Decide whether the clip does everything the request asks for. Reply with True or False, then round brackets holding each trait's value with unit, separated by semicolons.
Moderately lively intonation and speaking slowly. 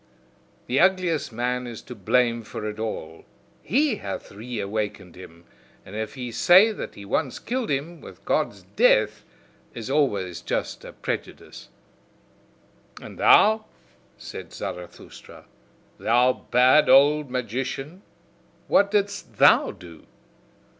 False (7.4 semitones; 120 wpm)